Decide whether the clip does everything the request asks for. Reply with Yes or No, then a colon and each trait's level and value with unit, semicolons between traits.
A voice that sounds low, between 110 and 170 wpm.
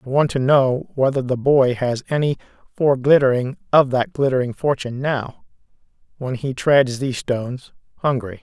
Yes: low, 130 Hz; average, 150 wpm